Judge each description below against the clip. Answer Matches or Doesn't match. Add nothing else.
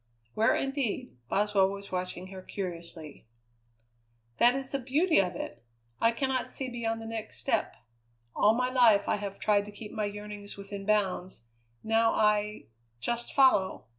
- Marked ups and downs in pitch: Doesn't match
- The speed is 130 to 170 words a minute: Matches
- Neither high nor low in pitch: Doesn't match